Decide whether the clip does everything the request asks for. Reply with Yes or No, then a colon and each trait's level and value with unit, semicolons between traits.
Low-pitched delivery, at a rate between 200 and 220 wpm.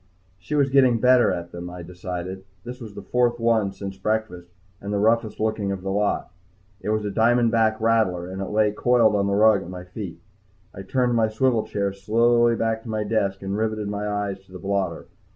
Yes: low, 105 Hz; fast, 205 wpm